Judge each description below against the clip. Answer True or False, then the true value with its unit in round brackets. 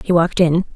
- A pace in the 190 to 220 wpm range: False (235 wpm)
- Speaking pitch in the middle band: True (170 Hz)